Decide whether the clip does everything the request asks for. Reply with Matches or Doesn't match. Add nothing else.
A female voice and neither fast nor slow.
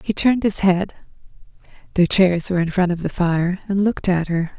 Matches